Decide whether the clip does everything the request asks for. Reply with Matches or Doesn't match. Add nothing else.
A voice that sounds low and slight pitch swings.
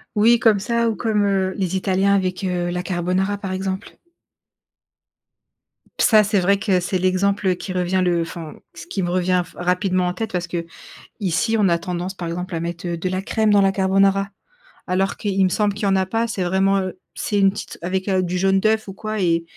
Doesn't match